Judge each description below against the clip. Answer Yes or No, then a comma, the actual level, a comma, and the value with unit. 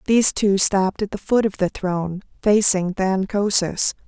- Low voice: No, high, 195 Hz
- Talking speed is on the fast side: No, average, 175 wpm